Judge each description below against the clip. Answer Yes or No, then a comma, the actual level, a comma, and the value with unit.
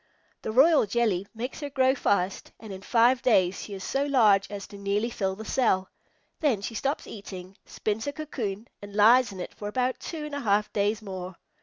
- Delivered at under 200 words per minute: No, fast, 205 wpm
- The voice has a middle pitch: No, high, 215 Hz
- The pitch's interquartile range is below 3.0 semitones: No, average, 4.5 semitones